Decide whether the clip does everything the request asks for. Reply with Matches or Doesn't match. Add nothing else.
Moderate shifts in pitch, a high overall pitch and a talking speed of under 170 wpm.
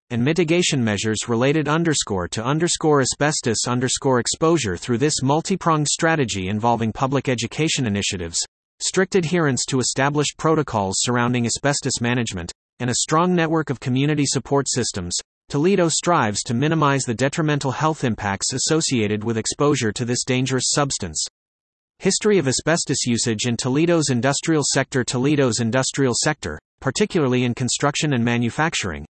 Doesn't match